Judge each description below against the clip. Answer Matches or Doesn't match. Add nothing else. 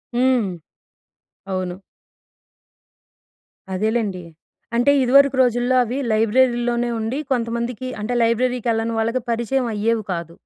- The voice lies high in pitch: Matches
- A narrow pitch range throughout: Matches